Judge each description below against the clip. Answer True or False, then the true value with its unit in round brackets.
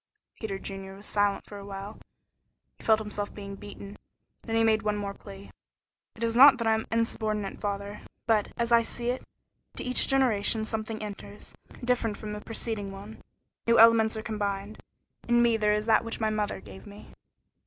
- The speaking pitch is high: True (215 Hz)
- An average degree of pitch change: False (2.0 semitones)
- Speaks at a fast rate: False (185 wpm)